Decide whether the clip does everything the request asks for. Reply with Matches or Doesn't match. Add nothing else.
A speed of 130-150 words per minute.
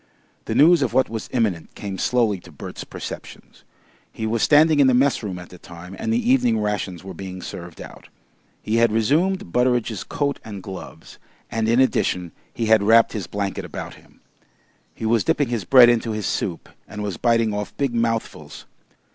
Doesn't match